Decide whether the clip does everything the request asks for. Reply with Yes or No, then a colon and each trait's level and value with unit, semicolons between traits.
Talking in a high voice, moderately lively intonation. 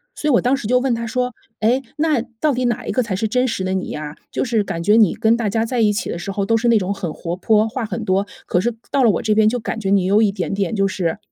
Yes: high, 220 Hz; average, 3.6 semitones